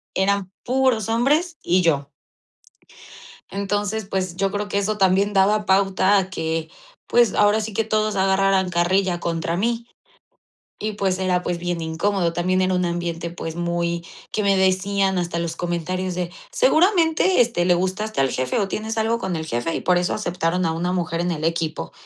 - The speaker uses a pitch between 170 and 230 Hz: Yes, medium, 185 Hz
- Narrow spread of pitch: No, average, 3.2 semitones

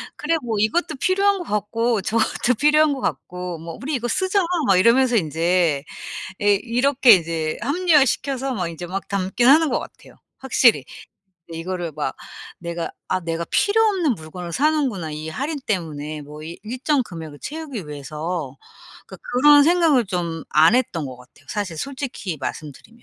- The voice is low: No, high, 205 Hz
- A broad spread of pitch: Yes, wide, 8.8 semitones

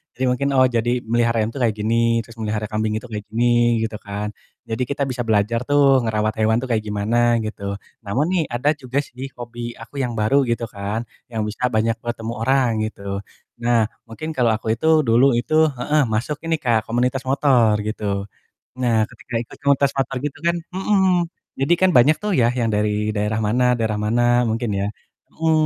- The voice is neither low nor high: No, low, 115 Hz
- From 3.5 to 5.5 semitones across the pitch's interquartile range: No, average, 3.1 semitones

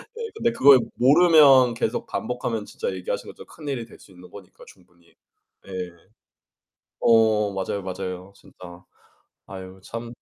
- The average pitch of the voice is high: No, low, 110 Hz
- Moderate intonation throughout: No, wide, 6.4 semitones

